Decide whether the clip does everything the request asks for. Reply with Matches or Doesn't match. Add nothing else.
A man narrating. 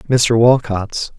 Matches